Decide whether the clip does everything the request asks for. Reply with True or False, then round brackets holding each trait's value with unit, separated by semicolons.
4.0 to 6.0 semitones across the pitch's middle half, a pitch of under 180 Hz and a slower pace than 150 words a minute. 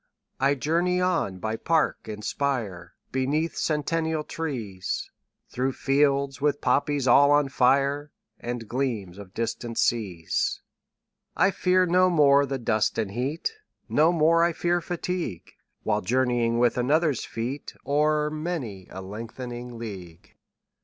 True (5.1 semitones; 135 Hz; 135 wpm)